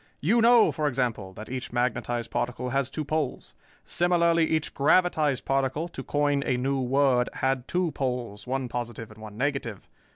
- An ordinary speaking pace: Yes, average, 165 wpm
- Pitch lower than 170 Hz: Yes, low, 135 Hz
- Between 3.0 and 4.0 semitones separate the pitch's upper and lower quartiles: Yes, average, 3.7 semitones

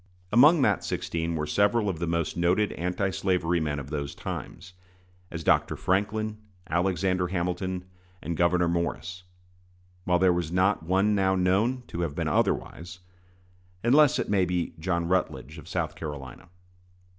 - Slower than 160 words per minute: Yes, average, 150 wpm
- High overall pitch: No, very low, 90 Hz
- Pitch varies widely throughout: No, narrow, 2.4 semitones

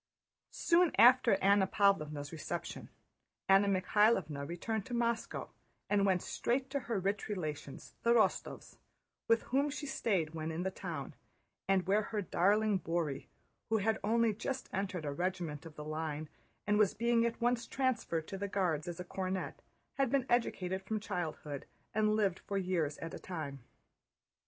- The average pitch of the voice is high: Yes, high, 195 Hz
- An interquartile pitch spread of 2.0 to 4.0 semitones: No, average, 5.0 semitones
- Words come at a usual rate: Yes, average, 160 wpm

